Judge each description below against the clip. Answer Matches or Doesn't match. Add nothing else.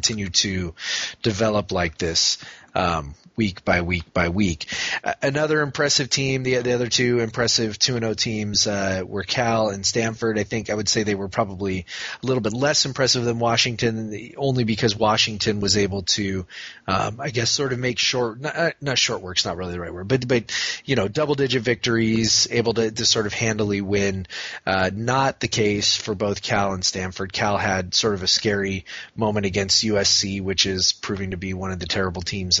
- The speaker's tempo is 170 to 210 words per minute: Matches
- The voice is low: Matches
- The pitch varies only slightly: Doesn't match